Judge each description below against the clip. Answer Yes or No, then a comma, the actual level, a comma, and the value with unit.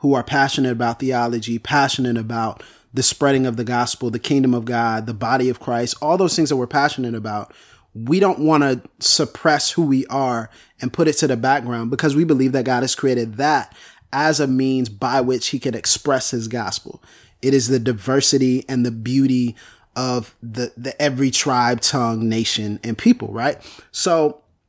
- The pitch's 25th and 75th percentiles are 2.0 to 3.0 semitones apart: Yes, average, 2.7 semitones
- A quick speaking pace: No, average, 185 wpm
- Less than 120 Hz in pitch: No, low, 130 Hz